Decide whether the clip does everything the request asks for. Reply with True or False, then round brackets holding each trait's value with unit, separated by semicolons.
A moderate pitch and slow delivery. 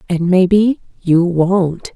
True (180 Hz; 125 wpm)